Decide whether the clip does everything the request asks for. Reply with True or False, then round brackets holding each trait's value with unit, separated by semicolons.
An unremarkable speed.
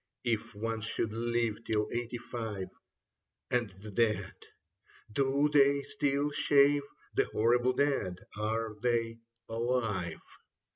False (115 wpm)